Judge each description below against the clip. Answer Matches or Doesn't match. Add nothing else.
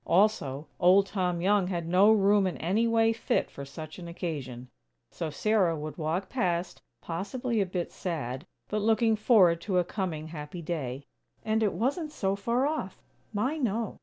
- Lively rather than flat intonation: Doesn't match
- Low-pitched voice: Doesn't match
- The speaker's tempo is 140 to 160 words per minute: Doesn't match